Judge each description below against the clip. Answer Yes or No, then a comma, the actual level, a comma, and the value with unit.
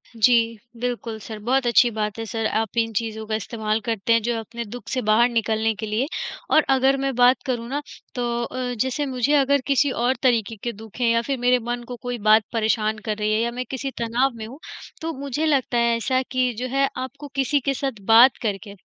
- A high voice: Yes, high, 240 Hz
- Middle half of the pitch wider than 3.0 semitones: No, average, 2.7 semitones